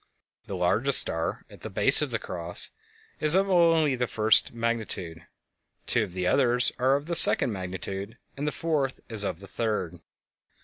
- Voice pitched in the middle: No, low, 115 Hz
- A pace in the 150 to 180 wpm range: Yes, average, 170 wpm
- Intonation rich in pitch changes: Yes, wide, 6.9 semitones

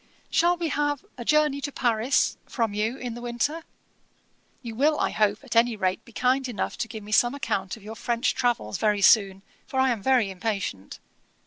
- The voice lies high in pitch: Yes, high, 235 Hz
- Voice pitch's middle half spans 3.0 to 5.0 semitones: Yes, average, 4.0 semitones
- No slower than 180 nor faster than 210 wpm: Yes, average, 200 wpm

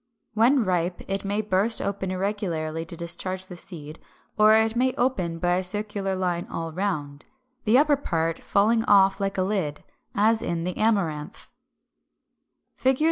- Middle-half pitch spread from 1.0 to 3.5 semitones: No, average, 3.9 semitones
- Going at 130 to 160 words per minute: Yes, average, 155 wpm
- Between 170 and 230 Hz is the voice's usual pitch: Yes, high, 190 Hz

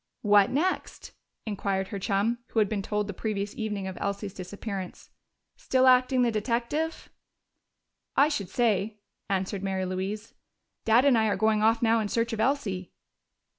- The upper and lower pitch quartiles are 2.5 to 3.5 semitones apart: Yes, average, 2.9 semitones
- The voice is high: Yes, high, 215 Hz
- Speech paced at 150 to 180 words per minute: Yes, average, 160 wpm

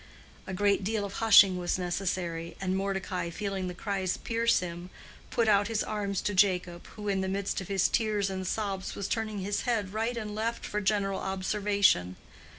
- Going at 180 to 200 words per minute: Yes, average, 185 wpm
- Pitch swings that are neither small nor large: No, narrow, 2.1 semitones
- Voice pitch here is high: Yes, high, 195 Hz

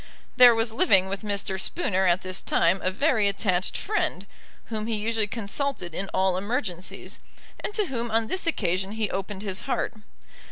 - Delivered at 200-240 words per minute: No, average, 170 wpm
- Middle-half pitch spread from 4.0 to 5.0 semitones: No, average, 3.4 semitones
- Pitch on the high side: Yes, high, 205 Hz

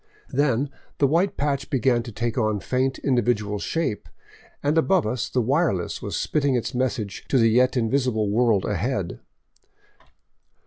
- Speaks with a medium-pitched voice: No, low, 125 Hz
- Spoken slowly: No, average, 145 wpm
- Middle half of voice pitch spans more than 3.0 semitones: Yes, average, 3.9 semitones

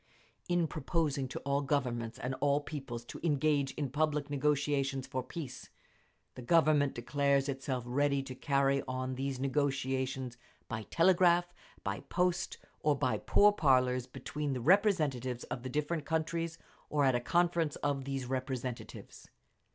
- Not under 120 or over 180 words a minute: Yes, average, 140 wpm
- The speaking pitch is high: No, medium, 140 Hz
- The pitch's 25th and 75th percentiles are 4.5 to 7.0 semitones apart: No, average, 2.8 semitones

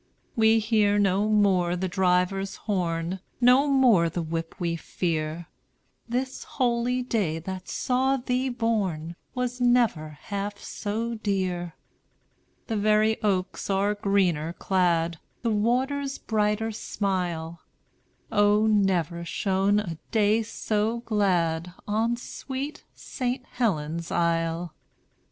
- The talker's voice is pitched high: Yes, high, 205 Hz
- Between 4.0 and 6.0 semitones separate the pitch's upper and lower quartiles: Yes, average, 4.7 semitones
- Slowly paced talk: Yes, slow, 110 wpm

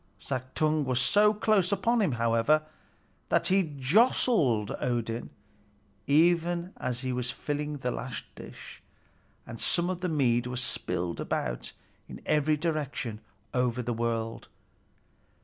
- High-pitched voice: No, low, 135 Hz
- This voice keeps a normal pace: No, slow, 130 wpm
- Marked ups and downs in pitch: Yes, wide, 6.1 semitones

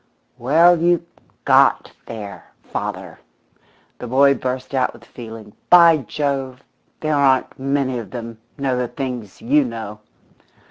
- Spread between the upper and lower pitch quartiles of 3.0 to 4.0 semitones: Yes, average, 3.4 semitones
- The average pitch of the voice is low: Yes, low, 130 Hz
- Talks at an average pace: No, slow, 130 wpm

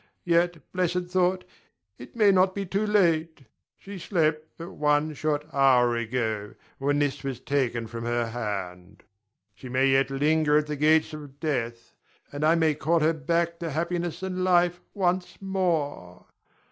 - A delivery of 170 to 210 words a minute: No, average, 160 wpm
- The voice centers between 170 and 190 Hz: No, medium, 155 Hz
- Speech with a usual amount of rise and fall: Yes, average, 4.6 semitones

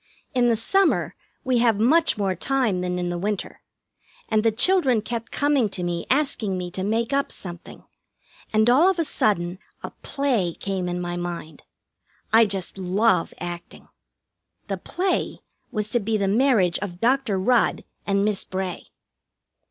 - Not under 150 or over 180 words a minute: Yes, average, 160 wpm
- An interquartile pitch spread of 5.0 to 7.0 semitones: Yes, wide, 5.4 semitones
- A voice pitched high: Yes, high, 210 Hz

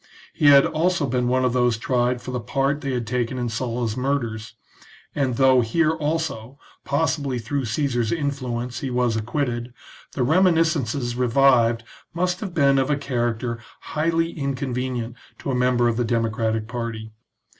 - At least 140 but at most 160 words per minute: Yes, average, 155 wpm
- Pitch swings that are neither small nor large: Yes, average, 3.1 semitones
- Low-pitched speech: Yes, low, 125 Hz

